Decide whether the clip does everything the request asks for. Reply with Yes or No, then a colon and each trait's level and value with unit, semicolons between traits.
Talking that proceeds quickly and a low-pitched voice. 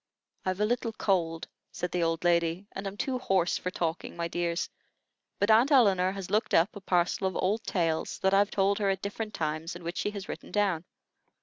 No: fast, 210 wpm; high, 190 Hz